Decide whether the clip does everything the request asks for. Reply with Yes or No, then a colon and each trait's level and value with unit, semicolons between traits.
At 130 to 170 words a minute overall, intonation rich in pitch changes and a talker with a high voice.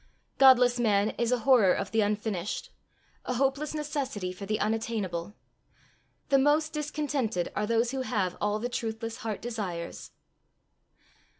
No: slow, 135 wpm; average, 4.2 semitones; high, 230 Hz